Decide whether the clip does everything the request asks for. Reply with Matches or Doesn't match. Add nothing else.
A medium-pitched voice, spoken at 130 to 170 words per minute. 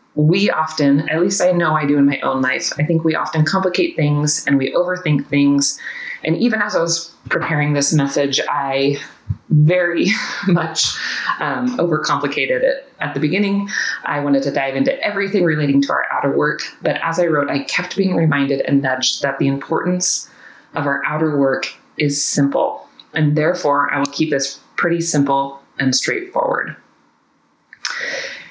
Matches